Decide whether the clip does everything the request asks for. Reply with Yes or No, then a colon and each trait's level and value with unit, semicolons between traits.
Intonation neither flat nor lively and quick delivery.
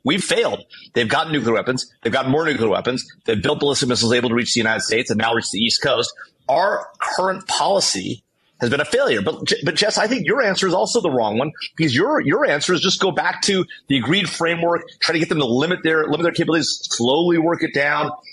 Yes: average, 4.8 semitones; fast, 235 wpm